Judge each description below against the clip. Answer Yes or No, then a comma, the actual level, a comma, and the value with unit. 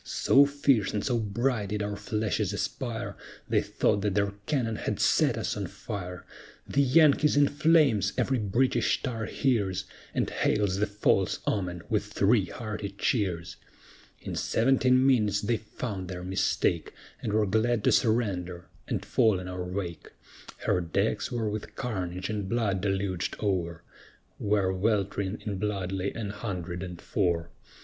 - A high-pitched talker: No, low, 105 Hz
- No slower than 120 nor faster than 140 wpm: No, average, 155 wpm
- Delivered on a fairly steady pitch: No, average, 3.5 semitones